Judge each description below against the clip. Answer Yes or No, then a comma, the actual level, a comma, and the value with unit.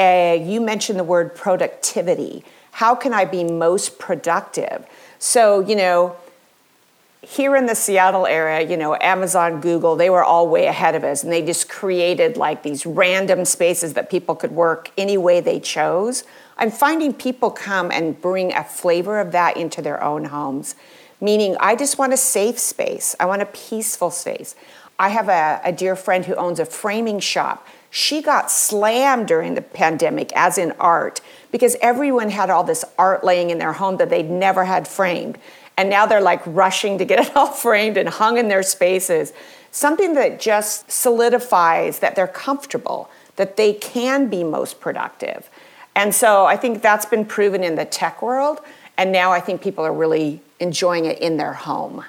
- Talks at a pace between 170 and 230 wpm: Yes, average, 180 wpm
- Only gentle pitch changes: No, average, 4.8 semitones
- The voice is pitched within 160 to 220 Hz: Yes, high, 190 Hz